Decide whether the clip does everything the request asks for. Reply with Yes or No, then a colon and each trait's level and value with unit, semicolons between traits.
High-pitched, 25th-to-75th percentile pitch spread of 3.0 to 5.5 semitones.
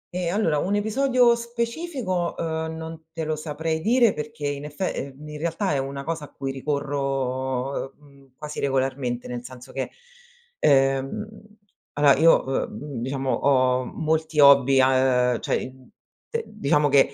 No: medium, 145 Hz; average, 3.3 semitones